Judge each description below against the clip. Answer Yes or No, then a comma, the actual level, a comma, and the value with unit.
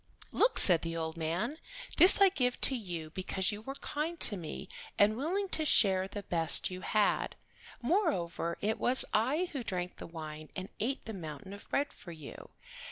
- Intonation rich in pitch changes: Yes, wide, 8.2 semitones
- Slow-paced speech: No, average, 185 wpm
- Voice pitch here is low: No, high, 205 Hz